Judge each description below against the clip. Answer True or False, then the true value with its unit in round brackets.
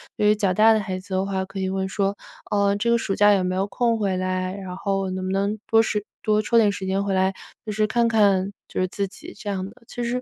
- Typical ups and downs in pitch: False (1.9 semitones)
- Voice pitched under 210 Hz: True (200 Hz)